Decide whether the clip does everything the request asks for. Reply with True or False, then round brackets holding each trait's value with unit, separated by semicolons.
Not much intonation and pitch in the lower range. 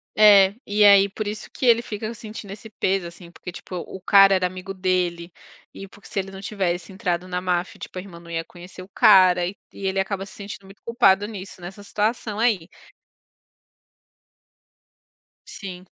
False (2.1 semitones; 195 Hz)